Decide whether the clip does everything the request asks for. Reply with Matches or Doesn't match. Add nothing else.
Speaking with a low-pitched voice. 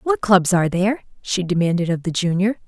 Doesn't match